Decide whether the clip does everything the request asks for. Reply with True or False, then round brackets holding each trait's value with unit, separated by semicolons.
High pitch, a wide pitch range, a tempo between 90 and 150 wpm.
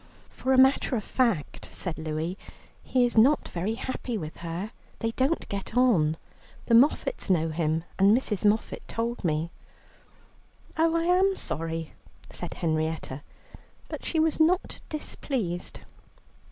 True (220 Hz; 8.2 semitones; 140 wpm)